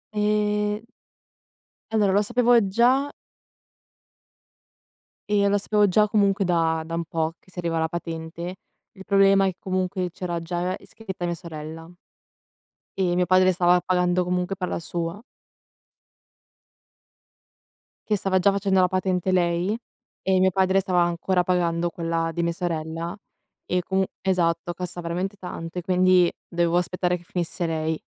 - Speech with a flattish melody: Yes, narrow, 2.2 semitones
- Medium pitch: Yes, medium, 180 Hz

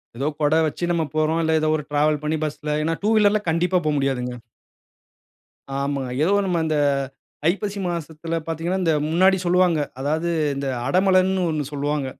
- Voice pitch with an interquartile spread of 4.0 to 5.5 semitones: No, average, 3.4 semitones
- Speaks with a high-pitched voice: No, medium, 160 Hz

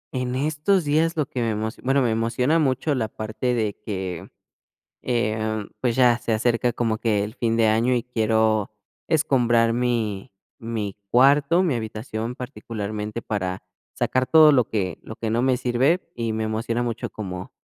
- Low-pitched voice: Yes, low, 115 Hz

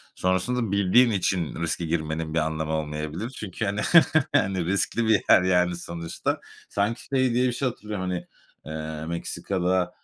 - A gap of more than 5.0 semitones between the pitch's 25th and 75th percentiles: No, average, 4.4 semitones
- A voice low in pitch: Yes, very low, 90 Hz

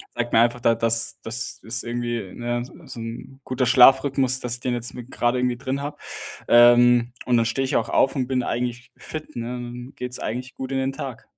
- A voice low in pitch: Yes, low, 120 Hz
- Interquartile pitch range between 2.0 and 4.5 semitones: No, narrow, 1.6 semitones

